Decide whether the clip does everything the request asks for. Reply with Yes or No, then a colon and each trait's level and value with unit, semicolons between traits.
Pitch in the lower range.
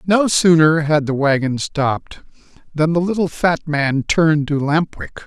No: medium, 155 Hz